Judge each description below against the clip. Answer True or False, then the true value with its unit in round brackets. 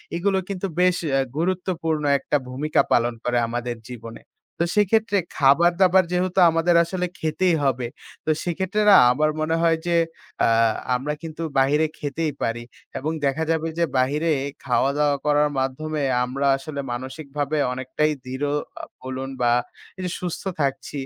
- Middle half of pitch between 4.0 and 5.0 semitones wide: True (4.3 semitones)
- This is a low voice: False (155 Hz)